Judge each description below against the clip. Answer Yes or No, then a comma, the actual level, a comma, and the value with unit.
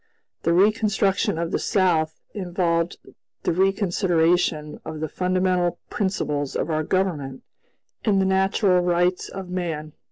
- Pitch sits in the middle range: Yes, medium, 180 Hz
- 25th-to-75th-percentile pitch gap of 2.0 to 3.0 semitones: Yes, average, 2.7 semitones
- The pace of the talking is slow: Yes, slow, 125 wpm